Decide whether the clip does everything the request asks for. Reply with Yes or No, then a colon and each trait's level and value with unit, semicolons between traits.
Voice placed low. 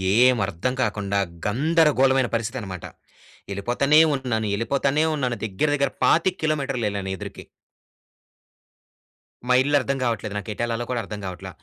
Yes: low, 120 Hz